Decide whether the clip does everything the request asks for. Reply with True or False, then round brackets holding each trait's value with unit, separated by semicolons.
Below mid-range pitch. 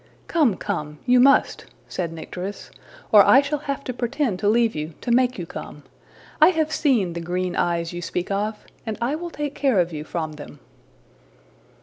False (210 Hz)